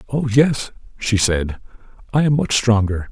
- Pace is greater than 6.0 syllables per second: No, 4.6 syllables/s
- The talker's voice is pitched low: Yes, low, 115 Hz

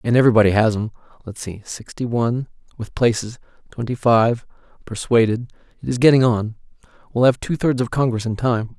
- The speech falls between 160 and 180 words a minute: Yes, average, 165 wpm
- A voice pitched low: Yes, low, 115 Hz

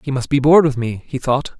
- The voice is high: No, low, 135 Hz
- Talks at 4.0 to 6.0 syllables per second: No, 6.4 syllables/s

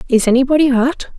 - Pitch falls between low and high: No, very high, 260 Hz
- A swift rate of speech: No, average, 150 wpm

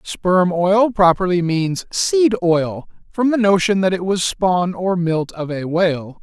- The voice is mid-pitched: Yes, medium, 180 Hz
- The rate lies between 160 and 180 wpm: Yes, average, 175 wpm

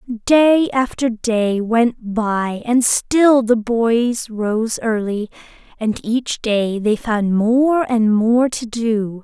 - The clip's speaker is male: No, female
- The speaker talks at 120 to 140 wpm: Yes, slow, 135 wpm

